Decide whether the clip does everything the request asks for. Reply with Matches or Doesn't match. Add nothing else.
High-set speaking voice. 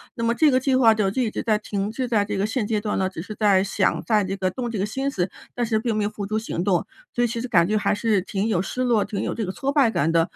Matches